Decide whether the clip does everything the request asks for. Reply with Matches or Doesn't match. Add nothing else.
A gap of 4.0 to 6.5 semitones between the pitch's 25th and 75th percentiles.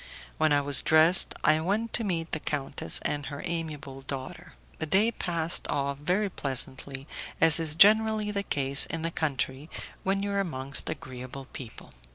Matches